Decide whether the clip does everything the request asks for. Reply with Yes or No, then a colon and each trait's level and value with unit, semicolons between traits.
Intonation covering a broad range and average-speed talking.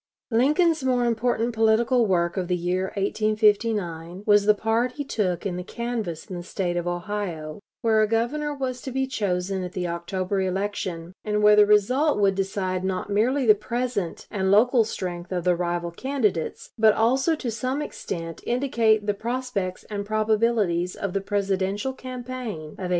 No: average, 4.5 semitones; average, 170 wpm